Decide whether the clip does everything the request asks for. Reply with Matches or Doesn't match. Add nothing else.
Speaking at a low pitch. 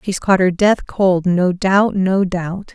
Doesn't match